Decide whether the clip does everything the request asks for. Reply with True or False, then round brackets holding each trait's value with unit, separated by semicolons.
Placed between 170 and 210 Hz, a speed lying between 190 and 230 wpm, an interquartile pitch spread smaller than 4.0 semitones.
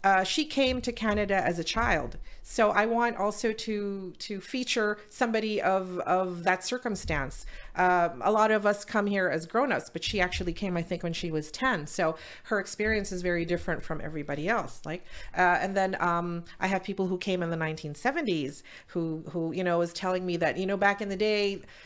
True (190 Hz; 205 wpm; 3.4 semitones)